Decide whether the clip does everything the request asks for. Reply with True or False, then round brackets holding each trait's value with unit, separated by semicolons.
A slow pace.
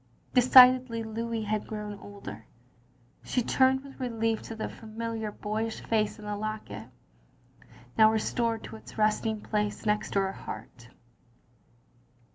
True (125 wpm)